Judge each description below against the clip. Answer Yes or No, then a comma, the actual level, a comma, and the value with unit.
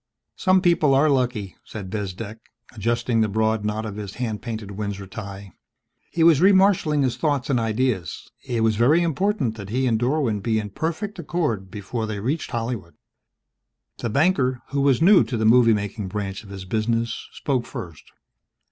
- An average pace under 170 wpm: No, average, 175 wpm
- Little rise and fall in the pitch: No, average, 5.0 semitones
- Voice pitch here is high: No, low, 115 Hz